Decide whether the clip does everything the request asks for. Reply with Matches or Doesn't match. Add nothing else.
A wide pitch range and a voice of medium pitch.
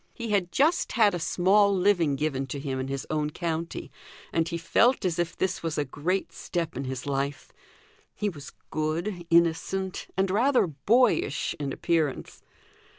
Doesn't match